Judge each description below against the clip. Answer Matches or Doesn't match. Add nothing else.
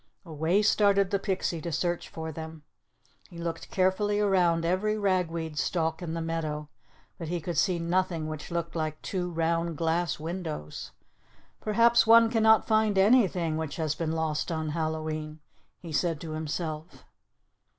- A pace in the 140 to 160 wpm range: Matches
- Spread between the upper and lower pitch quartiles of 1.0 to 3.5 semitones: Matches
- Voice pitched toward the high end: Doesn't match